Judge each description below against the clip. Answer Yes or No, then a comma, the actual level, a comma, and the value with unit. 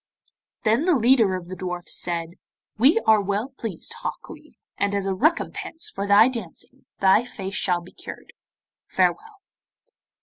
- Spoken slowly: No, average, 155 wpm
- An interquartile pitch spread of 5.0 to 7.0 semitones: Yes, wide, 5.4 semitones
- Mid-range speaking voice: No, high, 205 Hz